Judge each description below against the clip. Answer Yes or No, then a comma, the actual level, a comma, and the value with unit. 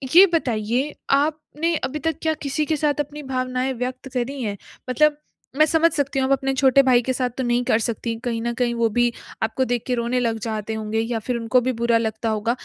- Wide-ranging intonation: No, average, 3.3 semitones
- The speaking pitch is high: Yes, very high, 250 Hz